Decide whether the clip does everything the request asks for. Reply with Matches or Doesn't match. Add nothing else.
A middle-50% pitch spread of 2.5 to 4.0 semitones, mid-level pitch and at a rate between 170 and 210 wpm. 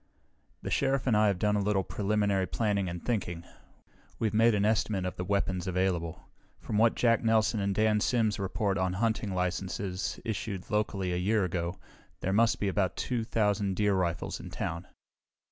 Doesn't match